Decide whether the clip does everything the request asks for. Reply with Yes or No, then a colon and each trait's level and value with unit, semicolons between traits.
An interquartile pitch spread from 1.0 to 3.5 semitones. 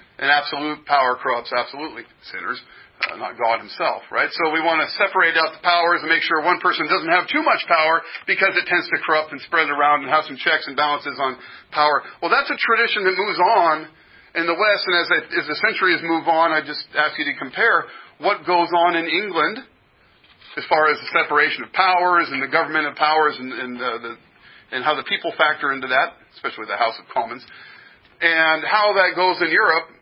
Yes: average, 2.9 semitones